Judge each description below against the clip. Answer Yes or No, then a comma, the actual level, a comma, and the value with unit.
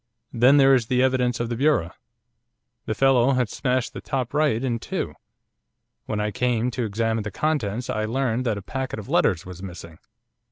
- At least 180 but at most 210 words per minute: Yes, average, 190 wpm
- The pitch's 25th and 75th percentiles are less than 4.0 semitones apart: Yes, average, 3.4 semitones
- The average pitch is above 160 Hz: No, low, 120 Hz